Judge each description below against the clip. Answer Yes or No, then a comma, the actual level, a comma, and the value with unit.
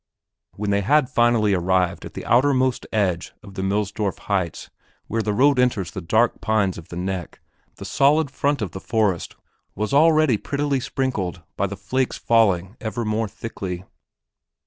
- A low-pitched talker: Yes, low, 105 Hz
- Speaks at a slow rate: No, average, 165 wpm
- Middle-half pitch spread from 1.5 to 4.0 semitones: No, average, 5.1 semitones